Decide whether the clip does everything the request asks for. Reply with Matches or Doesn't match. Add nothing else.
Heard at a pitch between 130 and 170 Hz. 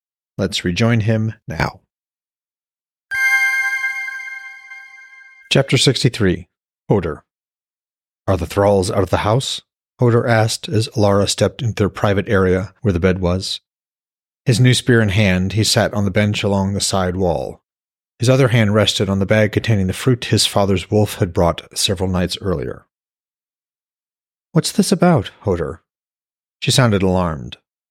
Doesn't match